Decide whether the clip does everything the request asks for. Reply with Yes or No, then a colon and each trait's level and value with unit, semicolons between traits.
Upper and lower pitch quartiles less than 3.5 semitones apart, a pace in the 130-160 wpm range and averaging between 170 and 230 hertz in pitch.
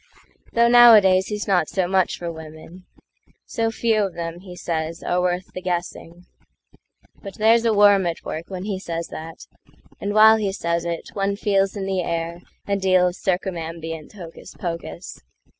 Yes: average, 3.0 semitones; average, 155 wpm; medium, 185 Hz